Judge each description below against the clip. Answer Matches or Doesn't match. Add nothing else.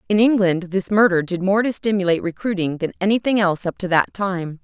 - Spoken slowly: Doesn't match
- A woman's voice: Matches